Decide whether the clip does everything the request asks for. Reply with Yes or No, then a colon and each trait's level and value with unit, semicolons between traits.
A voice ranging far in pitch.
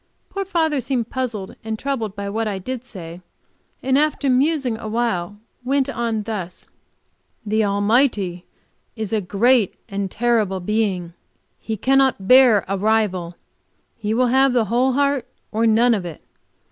No: average, 4.3 semitones